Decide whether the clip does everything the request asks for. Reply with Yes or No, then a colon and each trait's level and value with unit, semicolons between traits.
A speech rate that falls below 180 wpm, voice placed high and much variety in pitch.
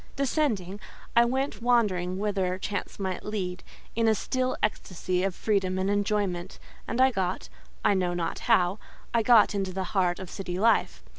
No: average, 155 wpm; high, 195 Hz; average, 3.6 semitones